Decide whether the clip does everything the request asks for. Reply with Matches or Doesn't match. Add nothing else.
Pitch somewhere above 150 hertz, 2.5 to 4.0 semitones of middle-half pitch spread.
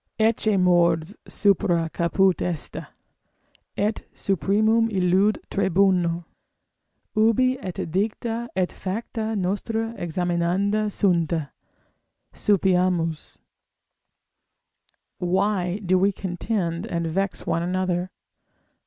Matches